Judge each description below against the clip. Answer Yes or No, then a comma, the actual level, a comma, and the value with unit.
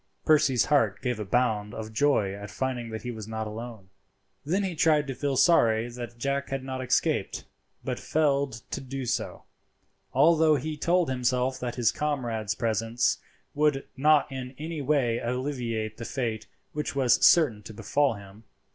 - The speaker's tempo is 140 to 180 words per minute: Yes, average, 165 wpm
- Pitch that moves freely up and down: No, average, 4.3 semitones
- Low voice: Yes, low, 125 Hz